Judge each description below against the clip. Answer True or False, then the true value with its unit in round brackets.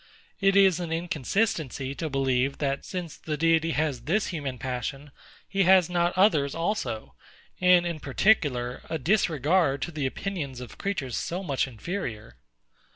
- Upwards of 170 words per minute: False (150 wpm)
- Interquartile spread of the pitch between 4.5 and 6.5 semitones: True (5.1 semitones)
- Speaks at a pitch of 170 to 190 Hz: False (160 Hz)